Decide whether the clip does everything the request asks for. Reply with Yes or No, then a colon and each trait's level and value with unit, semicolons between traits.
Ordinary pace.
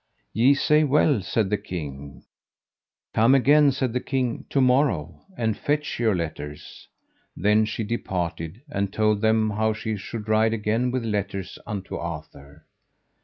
Yes: average, 145 wpm